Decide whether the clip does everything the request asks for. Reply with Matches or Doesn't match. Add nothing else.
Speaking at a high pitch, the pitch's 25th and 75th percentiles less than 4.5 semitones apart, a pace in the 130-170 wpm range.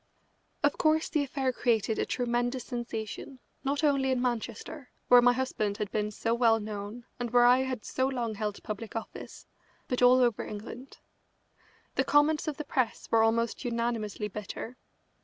Matches